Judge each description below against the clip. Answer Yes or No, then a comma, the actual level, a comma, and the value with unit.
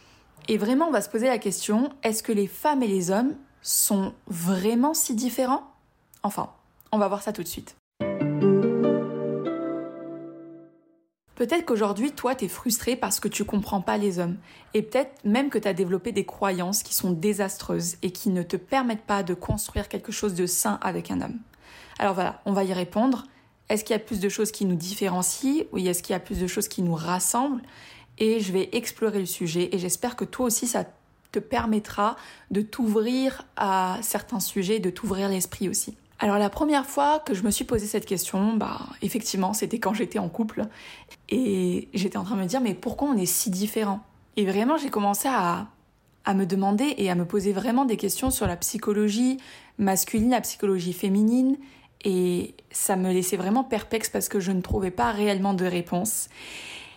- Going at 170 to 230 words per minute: Yes, average, 195 wpm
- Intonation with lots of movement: No, average, 3.5 semitones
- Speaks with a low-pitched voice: No, high, 205 Hz